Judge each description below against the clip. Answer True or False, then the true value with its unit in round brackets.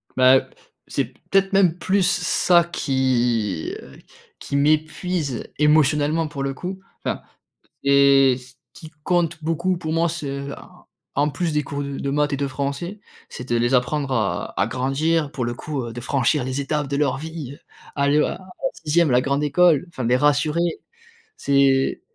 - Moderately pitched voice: True (145 Hz)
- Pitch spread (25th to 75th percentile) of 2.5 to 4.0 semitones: True (3.3 semitones)